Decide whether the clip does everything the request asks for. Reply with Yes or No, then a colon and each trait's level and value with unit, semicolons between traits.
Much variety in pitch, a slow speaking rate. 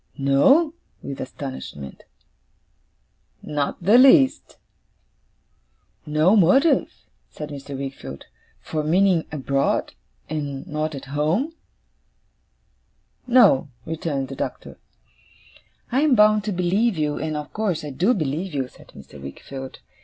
Yes: wide, 6.8 semitones; slow, 115 wpm